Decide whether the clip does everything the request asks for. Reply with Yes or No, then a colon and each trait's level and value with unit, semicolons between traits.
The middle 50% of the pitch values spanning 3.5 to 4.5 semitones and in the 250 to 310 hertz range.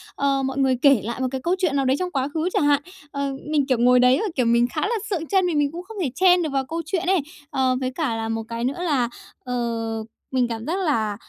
No: average, 4.9 semitones; very high, 275 Hz